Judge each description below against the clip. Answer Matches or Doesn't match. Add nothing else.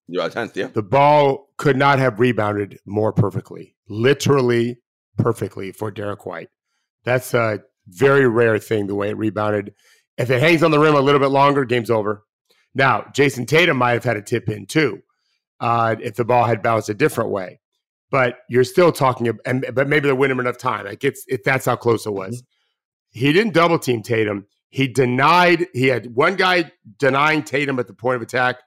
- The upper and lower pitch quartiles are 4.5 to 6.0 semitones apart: Doesn't match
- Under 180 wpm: Doesn't match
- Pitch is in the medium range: Doesn't match